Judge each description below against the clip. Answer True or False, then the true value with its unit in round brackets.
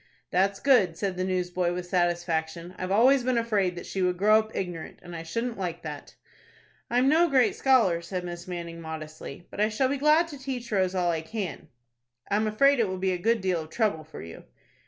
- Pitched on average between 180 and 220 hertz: True (185 Hz)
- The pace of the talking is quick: True (220 wpm)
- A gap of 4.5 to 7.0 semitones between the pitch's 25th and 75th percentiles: True (5.0 semitones)